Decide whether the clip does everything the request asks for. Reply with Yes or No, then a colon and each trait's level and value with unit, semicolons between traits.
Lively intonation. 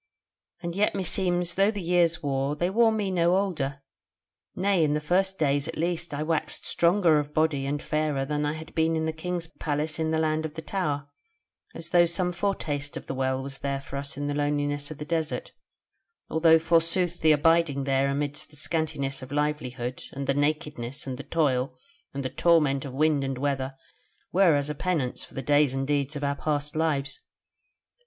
No: average, 3.1 semitones